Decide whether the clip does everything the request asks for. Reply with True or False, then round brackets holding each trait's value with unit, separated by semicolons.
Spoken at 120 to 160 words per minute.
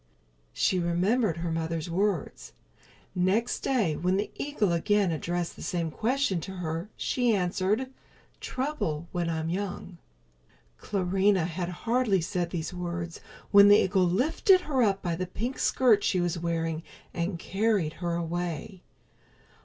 True (140 wpm)